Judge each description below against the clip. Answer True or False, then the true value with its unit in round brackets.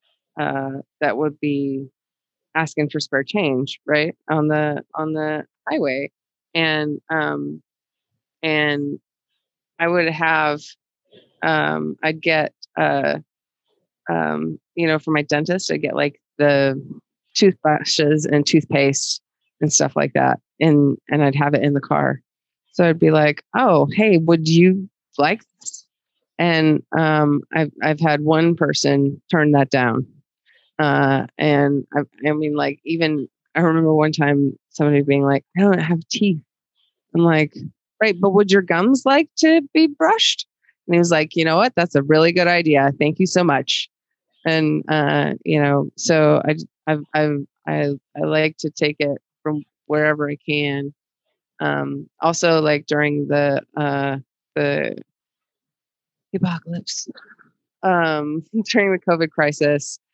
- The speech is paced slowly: False (145 wpm)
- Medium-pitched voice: True (150 Hz)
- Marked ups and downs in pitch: False (2.5 semitones)